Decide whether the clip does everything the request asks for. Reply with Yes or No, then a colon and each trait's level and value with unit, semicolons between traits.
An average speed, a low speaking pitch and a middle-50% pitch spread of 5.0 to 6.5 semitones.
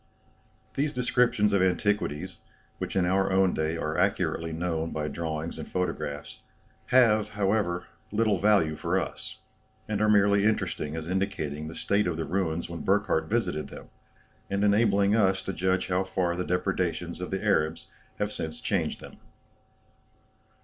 No: average, 155 wpm; very low, 95 Hz; average, 3.9 semitones